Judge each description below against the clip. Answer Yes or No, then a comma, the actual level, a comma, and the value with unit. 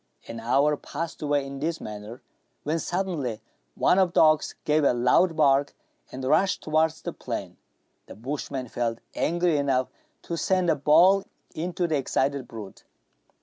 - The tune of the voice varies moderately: Yes, average, 4.3 semitones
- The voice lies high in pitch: No, medium, 150 Hz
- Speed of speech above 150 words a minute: Yes, average, 160 wpm